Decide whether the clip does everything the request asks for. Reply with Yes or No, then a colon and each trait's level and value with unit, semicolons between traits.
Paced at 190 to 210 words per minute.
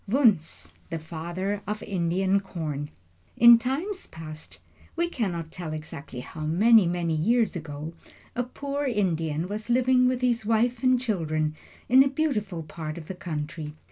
No: average, 150 wpm